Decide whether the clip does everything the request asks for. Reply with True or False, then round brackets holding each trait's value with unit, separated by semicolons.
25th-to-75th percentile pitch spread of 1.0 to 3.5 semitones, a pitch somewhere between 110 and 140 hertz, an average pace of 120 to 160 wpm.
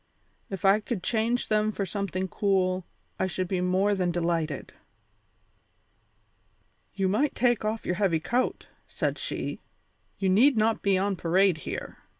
False (2.8 semitones; 195 Hz; 150 wpm)